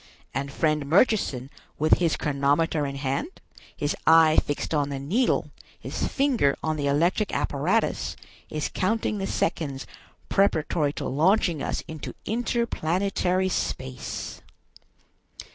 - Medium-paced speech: No, slow, 120 wpm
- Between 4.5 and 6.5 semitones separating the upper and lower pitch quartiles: Yes, average, 5.2 semitones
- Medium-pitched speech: Yes, medium, 155 Hz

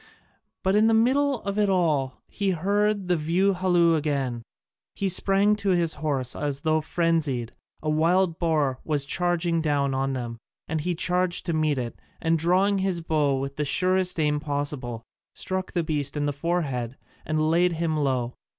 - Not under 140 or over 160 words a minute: No, average, 175 wpm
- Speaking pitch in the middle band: Yes, medium, 160 Hz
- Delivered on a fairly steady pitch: No, average, 4.2 semitones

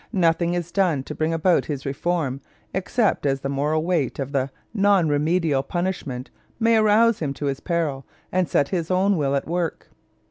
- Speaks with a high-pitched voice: No, medium, 165 Hz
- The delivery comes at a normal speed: Yes, average, 180 wpm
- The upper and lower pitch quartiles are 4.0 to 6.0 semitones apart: Yes, average, 4.6 semitones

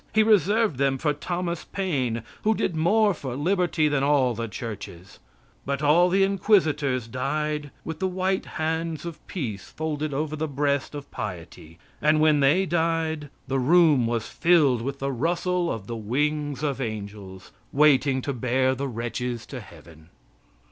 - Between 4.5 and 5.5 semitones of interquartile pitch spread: Yes, average, 4.8 semitones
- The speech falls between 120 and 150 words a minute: No, average, 160 wpm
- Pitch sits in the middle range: Yes, medium, 145 Hz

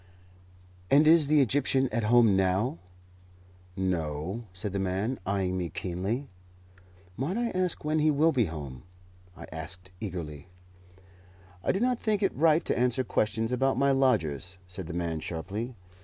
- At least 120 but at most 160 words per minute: Yes, average, 155 wpm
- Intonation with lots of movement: Yes, wide, 7.2 semitones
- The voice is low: Yes, low, 110 Hz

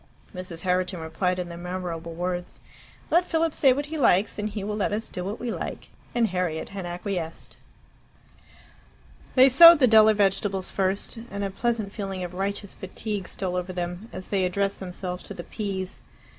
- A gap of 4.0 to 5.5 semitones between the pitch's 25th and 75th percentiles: No, average, 3.0 semitones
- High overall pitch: Yes, high, 195 Hz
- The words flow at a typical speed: Yes, average, 180 wpm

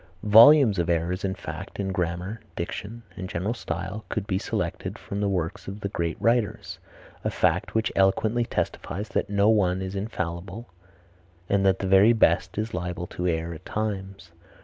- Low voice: Yes, very low, 95 Hz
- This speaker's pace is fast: No, average, 170 wpm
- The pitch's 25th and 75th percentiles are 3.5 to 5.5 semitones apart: No, average, 3.1 semitones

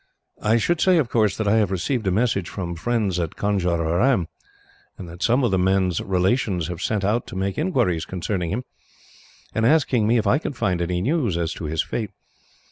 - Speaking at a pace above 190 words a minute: Yes, average, 200 wpm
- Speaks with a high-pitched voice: No, low, 100 Hz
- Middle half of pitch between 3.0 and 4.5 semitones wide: No, average, 4.9 semitones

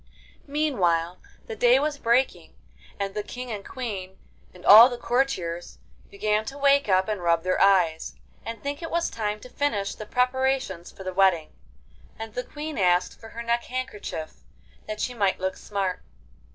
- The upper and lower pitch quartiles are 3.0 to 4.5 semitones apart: No, average, 5.3 semitones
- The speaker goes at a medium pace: Yes, average, 170 wpm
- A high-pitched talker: Yes, high, 215 Hz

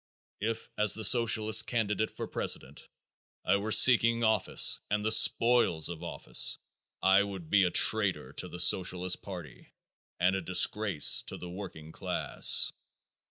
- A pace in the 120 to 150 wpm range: Yes, average, 145 wpm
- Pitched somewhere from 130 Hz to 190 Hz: No, low, 100 Hz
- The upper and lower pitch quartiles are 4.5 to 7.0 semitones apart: No, average, 3.4 semitones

